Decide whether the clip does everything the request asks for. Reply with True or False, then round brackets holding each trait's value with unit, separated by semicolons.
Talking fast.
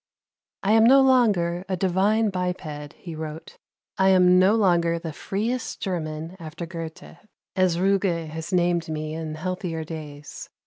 False (140 wpm)